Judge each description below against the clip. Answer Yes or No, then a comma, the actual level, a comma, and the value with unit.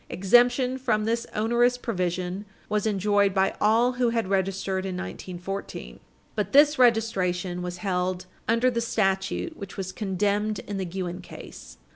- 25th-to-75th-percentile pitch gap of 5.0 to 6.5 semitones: No, average, 3.8 semitones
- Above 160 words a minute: No, average, 145 wpm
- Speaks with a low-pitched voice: No, high, 200 Hz